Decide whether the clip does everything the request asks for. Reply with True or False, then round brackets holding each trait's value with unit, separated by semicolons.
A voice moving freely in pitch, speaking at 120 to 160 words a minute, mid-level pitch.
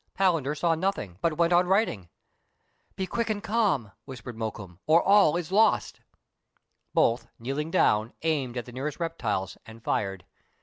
False (8.0 semitones; 170 wpm; 150 Hz)